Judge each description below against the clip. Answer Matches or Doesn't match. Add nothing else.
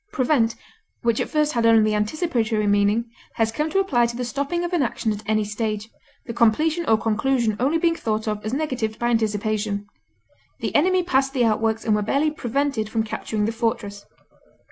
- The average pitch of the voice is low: Doesn't match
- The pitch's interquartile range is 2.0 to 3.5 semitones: Doesn't match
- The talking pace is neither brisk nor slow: Matches